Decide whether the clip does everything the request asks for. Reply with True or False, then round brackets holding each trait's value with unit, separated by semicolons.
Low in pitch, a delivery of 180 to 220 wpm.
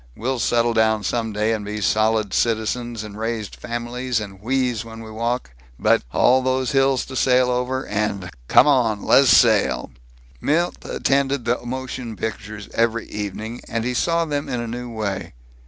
False (115 Hz; 170 wpm)